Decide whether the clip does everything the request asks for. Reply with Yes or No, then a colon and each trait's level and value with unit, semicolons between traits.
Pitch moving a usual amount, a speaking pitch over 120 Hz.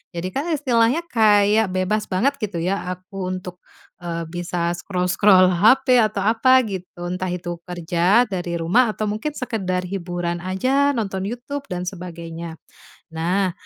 Yes: average, 4.0 semitones; high, 190 Hz